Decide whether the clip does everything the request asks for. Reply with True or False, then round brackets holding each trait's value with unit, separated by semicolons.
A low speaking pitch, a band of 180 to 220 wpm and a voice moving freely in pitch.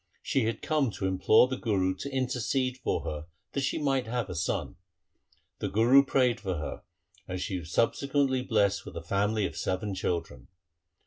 True (110 Hz; 185 wpm; 5.7 semitones)